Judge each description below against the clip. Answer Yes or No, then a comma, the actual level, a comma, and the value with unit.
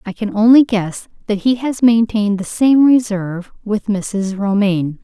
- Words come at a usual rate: Yes, average, 165 wpm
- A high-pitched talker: Yes, high, 210 Hz